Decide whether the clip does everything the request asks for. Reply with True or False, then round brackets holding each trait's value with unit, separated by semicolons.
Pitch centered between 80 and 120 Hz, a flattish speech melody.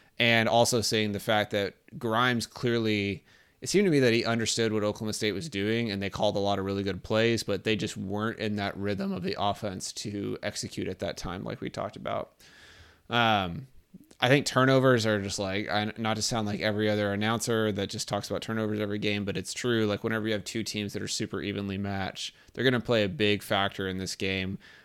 True (105 Hz; 2.1 semitones)